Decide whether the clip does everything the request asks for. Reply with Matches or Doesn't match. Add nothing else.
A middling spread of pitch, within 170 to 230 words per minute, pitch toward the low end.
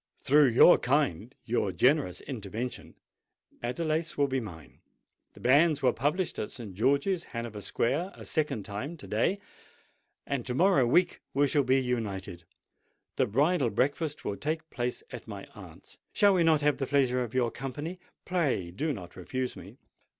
Doesn't match